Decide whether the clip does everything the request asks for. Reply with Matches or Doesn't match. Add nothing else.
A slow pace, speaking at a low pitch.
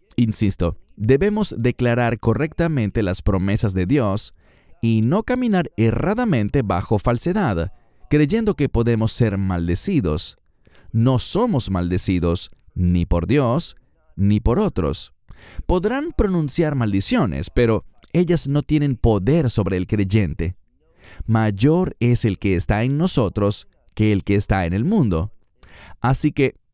Matches